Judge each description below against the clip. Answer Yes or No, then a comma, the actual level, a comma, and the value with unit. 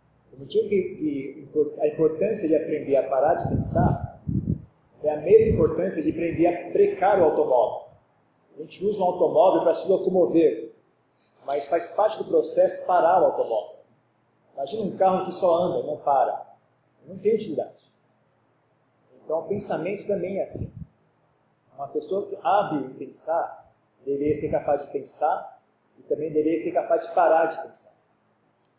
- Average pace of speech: Yes, average, 150 wpm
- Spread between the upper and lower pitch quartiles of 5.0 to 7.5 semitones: Yes, wide, 5.4 semitones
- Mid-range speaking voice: Yes, medium, 180 Hz